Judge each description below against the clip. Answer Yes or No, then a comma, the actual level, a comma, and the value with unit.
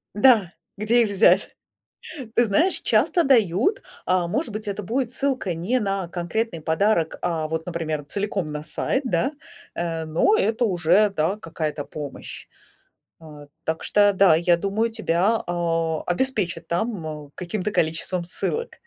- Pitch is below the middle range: No, medium, 185 Hz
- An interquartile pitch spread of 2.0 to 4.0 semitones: No, average, 5.0 semitones